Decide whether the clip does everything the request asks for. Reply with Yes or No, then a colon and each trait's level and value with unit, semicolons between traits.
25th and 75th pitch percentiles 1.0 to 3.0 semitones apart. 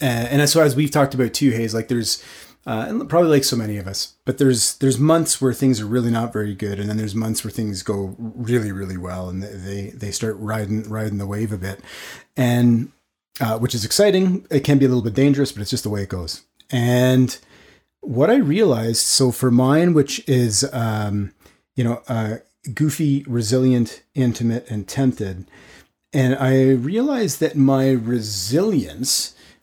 No: average, 3.9 semitones